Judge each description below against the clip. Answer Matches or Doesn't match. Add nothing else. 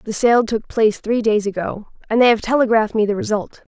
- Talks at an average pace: Doesn't match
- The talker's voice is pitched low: Doesn't match